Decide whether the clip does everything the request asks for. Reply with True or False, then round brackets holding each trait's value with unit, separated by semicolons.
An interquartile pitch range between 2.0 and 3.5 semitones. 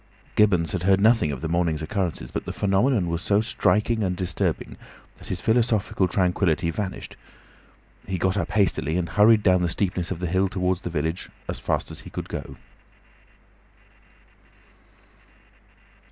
True (3.2 semitones)